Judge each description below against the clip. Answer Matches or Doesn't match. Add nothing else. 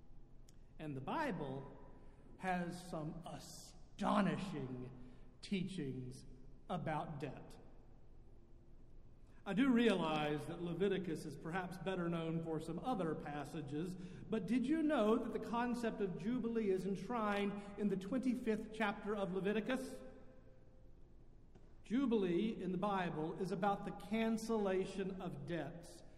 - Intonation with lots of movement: Matches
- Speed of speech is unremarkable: Doesn't match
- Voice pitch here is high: Doesn't match